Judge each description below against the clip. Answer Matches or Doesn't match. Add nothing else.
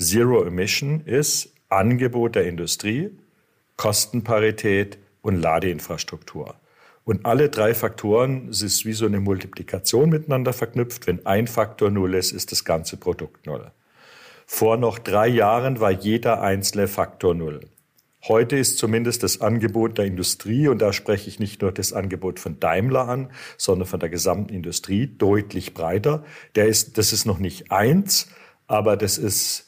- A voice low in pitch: Matches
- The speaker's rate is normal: Matches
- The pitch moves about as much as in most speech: Matches